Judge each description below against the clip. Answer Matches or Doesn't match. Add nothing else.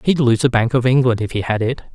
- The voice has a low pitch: Matches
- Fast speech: Matches